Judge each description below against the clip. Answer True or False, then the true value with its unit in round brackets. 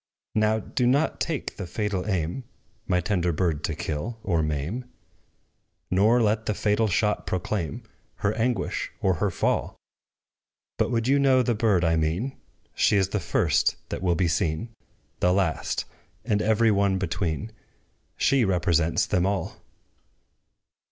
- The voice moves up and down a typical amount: True (4.4 semitones)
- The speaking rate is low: False (145 wpm)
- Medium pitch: False (100 Hz)